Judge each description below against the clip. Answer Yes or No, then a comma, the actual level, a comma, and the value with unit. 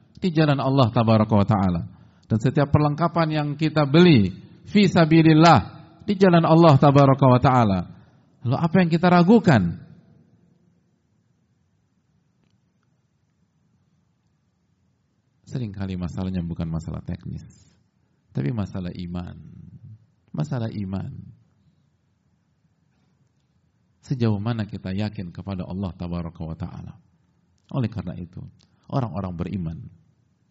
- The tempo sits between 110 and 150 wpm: No, average, 90 wpm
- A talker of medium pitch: No, low, 115 Hz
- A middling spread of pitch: No, wide, 8.1 semitones